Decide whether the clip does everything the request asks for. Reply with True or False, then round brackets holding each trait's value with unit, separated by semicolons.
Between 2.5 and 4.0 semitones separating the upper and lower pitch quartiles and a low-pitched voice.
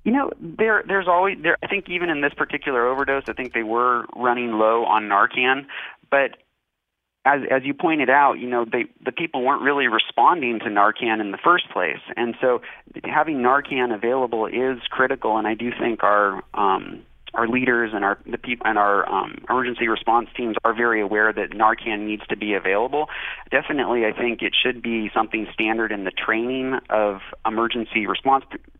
True (3.0 semitones; 120 Hz)